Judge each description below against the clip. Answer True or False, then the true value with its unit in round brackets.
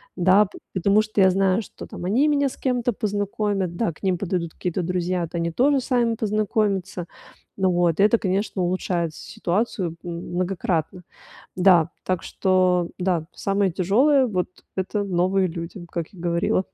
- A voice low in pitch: False (190 Hz)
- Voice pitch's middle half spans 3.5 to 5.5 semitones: False (3.0 semitones)